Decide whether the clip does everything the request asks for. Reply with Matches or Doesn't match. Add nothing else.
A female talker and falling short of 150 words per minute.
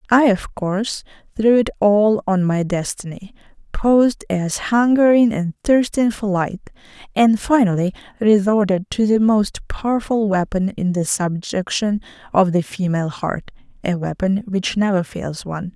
Matches